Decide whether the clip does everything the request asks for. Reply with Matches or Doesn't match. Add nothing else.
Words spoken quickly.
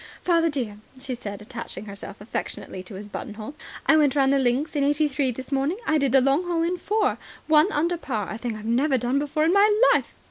Matches